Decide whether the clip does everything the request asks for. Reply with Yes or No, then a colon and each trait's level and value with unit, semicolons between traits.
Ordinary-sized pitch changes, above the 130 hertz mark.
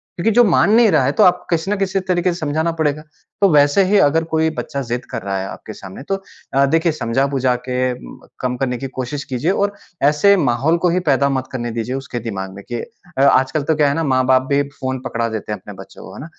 Yes: average, 4.5 semitones; medium, 140 Hz